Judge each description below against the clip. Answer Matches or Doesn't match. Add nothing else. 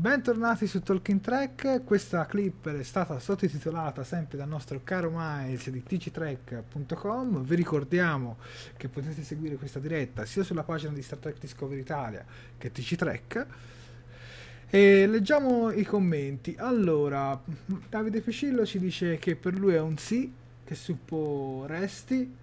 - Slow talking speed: Doesn't match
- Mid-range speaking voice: Matches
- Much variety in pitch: Matches